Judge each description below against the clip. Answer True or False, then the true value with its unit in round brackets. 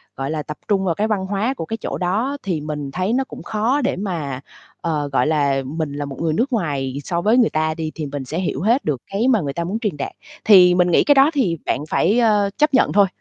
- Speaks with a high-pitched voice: False (180 Hz)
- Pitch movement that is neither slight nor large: False (6.4 semitones)